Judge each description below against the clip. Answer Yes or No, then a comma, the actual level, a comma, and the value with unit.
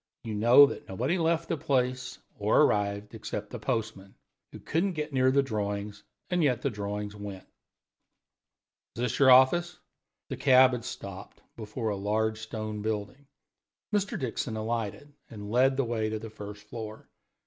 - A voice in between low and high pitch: No, low, 110 Hz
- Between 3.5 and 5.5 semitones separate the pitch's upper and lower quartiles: Yes, average, 4.0 semitones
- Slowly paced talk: No, average, 160 wpm